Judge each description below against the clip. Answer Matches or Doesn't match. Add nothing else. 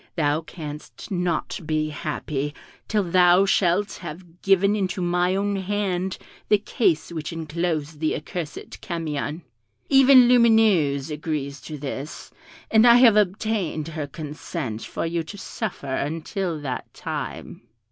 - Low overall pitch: Doesn't match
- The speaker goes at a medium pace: Doesn't match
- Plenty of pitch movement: Doesn't match